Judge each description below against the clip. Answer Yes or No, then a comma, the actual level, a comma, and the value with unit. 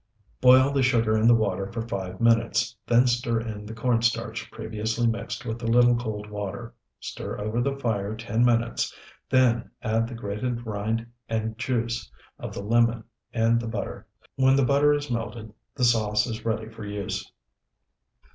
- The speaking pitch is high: No, low, 115 Hz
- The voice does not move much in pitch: Yes, narrow, 1.7 semitones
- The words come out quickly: No, average, 170 wpm